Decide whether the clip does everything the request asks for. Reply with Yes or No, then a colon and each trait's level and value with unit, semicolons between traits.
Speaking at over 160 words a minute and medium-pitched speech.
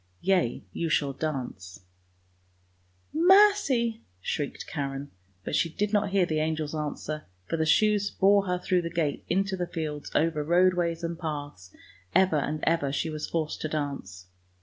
Yes: average, 170 wpm; medium, 160 Hz